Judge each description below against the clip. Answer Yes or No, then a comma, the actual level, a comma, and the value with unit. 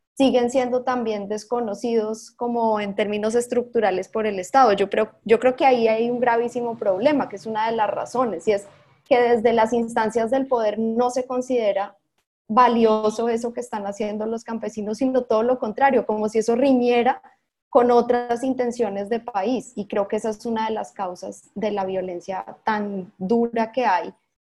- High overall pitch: Yes, high, 230 Hz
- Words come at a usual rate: Yes, average, 180 wpm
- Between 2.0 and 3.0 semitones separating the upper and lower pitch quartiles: Yes, narrow, 2.5 semitones